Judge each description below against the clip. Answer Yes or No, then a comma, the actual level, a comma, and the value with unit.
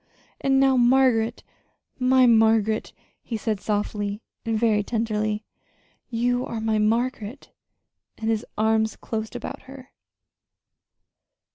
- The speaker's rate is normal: No, slow, 110 wpm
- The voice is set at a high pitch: Yes, high, 225 Hz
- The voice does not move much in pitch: Yes, narrow, 2.2 semitones